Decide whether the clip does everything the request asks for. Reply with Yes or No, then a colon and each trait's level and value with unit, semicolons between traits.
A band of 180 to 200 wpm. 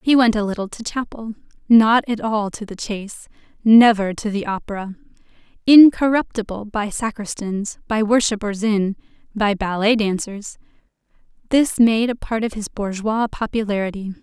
No: average, 140 wpm